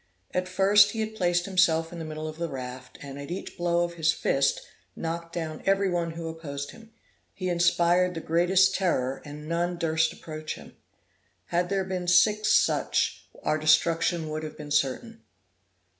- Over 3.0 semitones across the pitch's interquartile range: No, average, 2.7 semitones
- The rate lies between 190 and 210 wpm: No, average, 175 wpm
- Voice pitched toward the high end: No, medium, 170 Hz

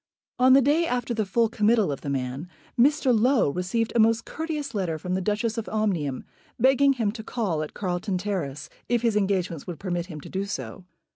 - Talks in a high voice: Yes, high, 210 Hz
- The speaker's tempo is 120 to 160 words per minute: No, fast, 205 wpm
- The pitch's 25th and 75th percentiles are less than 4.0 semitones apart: No, average, 5.0 semitones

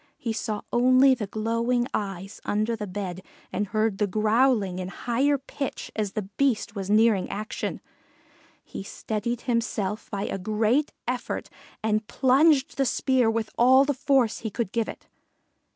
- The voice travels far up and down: No, average, 3.4 semitones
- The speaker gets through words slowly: No, average, 155 wpm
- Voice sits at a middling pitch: No, high, 225 Hz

